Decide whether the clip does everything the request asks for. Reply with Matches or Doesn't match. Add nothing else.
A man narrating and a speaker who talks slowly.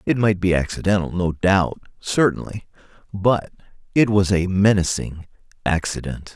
Matches